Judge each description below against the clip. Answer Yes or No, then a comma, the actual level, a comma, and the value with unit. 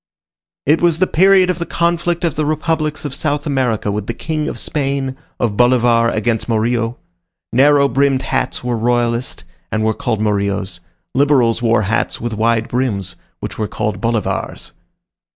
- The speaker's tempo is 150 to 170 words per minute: Yes, average, 160 wpm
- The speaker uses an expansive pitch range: No, average, 4.7 semitones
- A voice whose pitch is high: No, low, 125 Hz